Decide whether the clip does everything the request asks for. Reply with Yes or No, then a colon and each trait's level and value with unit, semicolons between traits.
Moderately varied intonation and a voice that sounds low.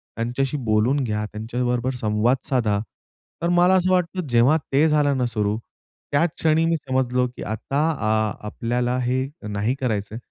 Yes: average, 4.6 semitones; low, 125 Hz